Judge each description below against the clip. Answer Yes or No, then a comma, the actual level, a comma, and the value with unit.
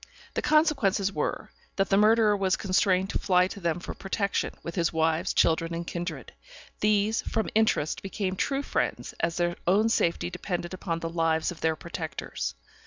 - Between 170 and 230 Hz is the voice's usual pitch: Yes, medium, 185 Hz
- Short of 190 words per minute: Yes, average, 175 wpm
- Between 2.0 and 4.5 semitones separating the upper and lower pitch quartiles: Yes, average, 3.2 semitones